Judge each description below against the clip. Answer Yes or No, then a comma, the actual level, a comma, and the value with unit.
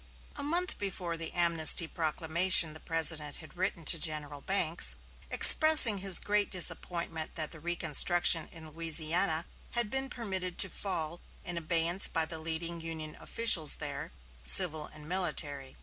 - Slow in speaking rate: No, average, 145 wpm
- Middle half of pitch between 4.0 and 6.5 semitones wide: No, average, 2.8 semitones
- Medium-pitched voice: Yes, medium, 170 Hz